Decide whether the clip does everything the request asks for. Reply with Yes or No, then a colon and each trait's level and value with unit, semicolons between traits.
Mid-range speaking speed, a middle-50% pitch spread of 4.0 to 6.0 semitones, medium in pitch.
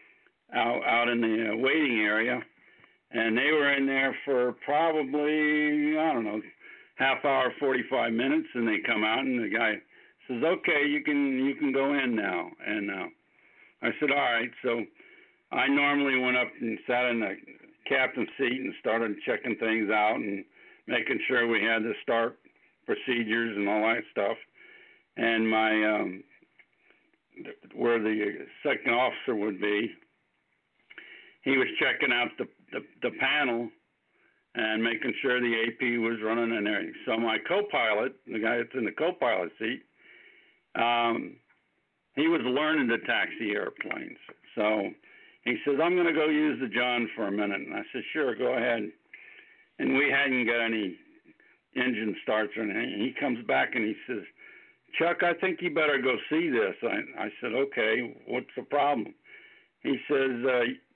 No: average, 160 wpm; average, 4.9 semitones; low, 125 Hz